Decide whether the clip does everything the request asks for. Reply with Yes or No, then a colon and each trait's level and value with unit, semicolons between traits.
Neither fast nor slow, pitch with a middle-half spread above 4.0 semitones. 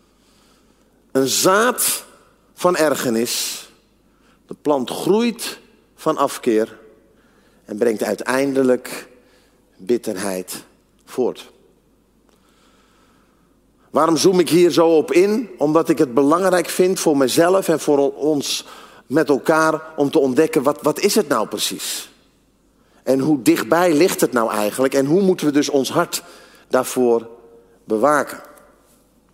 No: slow, 120 wpm; average, 5.3 semitones